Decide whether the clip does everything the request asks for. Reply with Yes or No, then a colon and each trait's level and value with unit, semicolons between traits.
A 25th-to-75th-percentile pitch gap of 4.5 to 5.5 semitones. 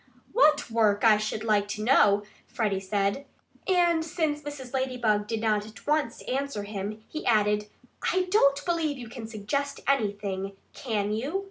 Yes: average, 5.2 semitones